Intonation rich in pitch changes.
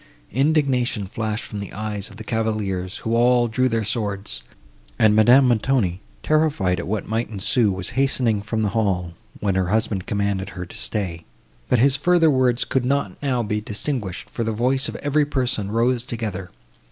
No: average, 4.0 semitones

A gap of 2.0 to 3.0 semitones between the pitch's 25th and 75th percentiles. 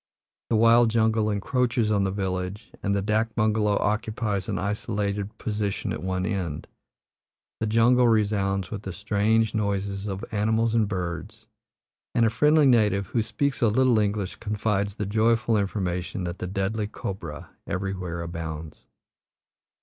Yes: narrow, 2.4 semitones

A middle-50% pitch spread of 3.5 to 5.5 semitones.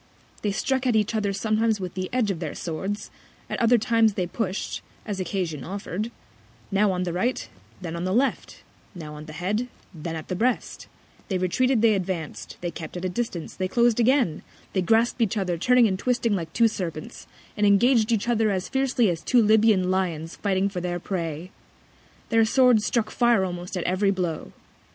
Yes: average, 4.2 semitones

